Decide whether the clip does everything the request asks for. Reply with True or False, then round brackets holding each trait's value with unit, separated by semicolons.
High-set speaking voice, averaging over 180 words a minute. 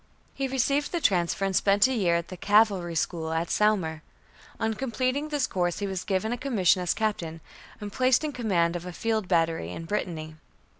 True (195 Hz; 195 wpm)